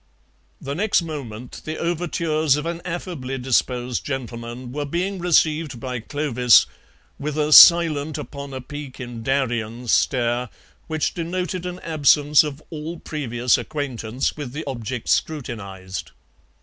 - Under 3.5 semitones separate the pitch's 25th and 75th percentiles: No, average, 4.2 semitones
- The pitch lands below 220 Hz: Yes, medium, 140 Hz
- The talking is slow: Yes, slow, 130 wpm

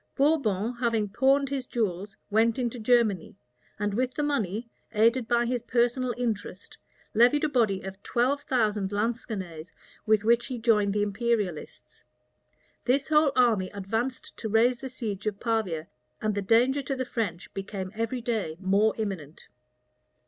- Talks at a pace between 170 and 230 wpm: No, average, 150 wpm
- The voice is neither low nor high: No, high, 225 Hz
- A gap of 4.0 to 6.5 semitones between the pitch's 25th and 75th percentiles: No, average, 3.5 semitones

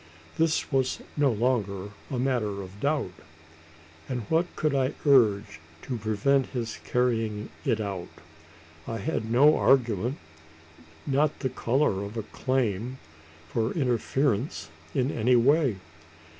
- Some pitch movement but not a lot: Yes, average, 4.1 semitones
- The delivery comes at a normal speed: No, slow, 125 wpm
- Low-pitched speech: Yes, low, 125 Hz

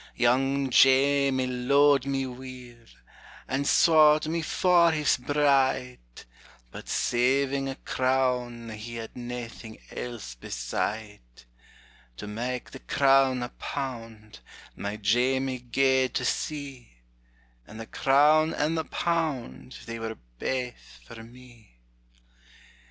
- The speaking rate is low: Yes, slow, 110 wpm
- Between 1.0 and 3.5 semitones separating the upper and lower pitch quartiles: Yes, average, 2.8 semitones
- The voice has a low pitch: Yes, low, 130 Hz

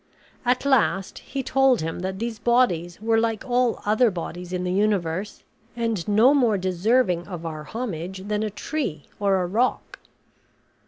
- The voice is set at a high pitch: Yes, high, 205 Hz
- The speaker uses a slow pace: No, average, 160 wpm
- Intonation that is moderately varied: Yes, average, 4.9 semitones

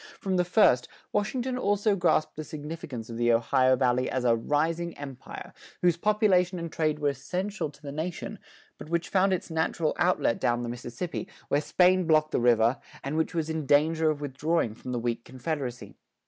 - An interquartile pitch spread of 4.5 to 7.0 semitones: Yes, wide, 5.5 semitones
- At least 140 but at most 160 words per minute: No, average, 185 wpm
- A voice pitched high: No, medium, 155 Hz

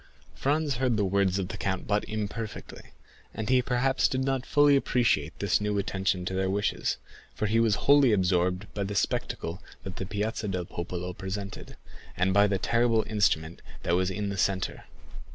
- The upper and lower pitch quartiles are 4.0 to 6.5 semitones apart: No, average, 3.4 semitones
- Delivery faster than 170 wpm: Yes, average, 180 wpm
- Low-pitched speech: Yes, low, 100 Hz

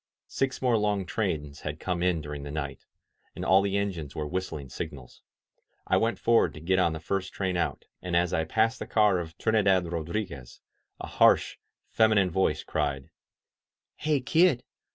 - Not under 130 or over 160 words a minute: No, average, 175 wpm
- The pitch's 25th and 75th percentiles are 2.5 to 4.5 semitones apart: No, average, 5.2 semitones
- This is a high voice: No, very low, 90 Hz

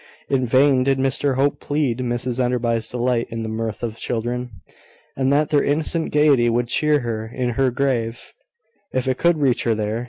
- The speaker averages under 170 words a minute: No, average, 185 wpm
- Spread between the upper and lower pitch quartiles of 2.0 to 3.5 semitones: Yes, average, 2.8 semitones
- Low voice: Yes, low, 125 Hz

